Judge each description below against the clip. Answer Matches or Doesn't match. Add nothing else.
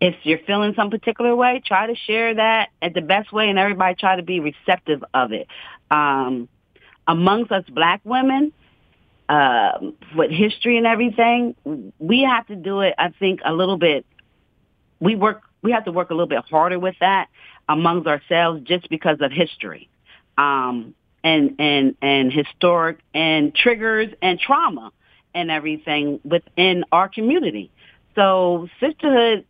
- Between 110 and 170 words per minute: Matches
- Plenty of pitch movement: Matches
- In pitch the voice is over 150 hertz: Matches